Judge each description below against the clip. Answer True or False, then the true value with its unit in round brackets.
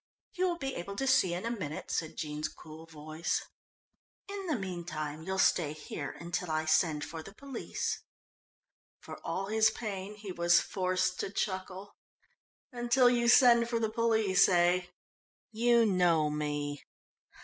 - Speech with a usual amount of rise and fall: False (6.2 semitones)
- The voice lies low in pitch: False (185 Hz)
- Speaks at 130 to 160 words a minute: True (150 wpm)